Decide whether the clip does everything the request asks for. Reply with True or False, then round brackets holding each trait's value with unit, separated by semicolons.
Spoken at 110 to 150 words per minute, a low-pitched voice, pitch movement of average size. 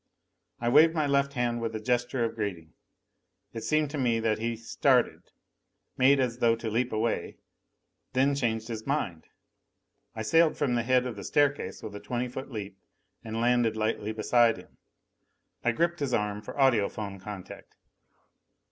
False (170 wpm; 120 Hz; 3.3 semitones)